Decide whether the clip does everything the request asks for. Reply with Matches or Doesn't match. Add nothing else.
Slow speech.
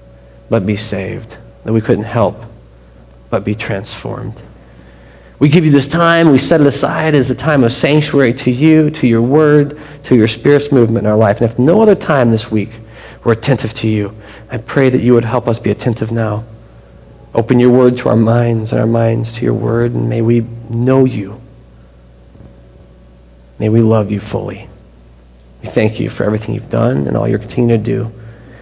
Doesn't match